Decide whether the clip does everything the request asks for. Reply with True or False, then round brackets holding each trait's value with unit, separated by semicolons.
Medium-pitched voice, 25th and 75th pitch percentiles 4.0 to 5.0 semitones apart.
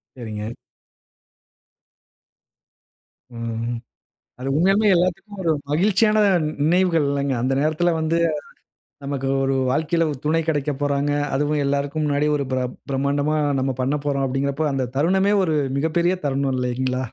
False (145 Hz; 3.4 semitones)